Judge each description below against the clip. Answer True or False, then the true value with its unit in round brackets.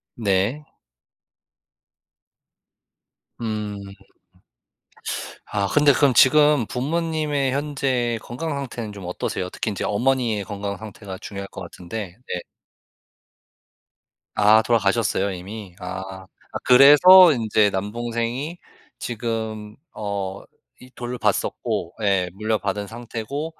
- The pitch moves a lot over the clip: False (4.9 semitones)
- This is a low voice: True (110 Hz)